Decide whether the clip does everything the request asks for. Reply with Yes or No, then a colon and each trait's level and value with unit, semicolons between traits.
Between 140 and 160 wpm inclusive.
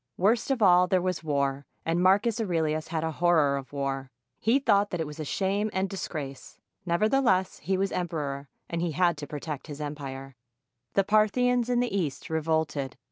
No: average, 190 wpm